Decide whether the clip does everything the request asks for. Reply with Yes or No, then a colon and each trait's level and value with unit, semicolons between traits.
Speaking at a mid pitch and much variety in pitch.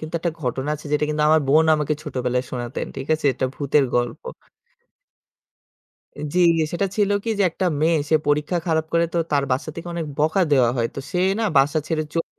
No: medium, 150 Hz; average, 3.4 semitones